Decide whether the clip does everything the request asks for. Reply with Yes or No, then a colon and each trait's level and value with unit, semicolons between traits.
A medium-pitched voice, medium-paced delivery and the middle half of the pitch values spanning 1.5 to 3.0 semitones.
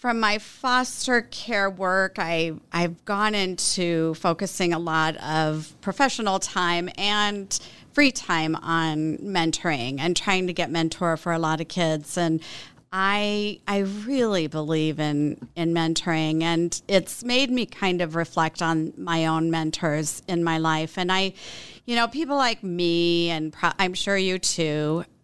No: medium, 170 Hz; average, 155 wpm; average, 3.5 semitones